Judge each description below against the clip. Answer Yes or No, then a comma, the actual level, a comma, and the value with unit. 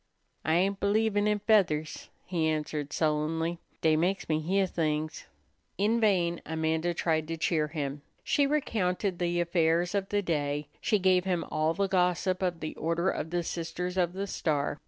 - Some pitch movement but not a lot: Yes, average, 3.2 semitones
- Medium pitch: Yes, medium, 170 Hz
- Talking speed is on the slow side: No, average, 170 wpm